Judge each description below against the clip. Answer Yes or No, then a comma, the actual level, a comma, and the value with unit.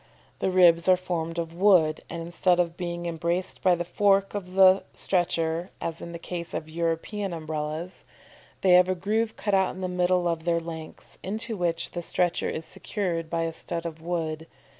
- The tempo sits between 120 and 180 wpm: No, average, 190 wpm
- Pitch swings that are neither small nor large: No, narrow, 1.9 semitones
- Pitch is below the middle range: No, medium, 175 Hz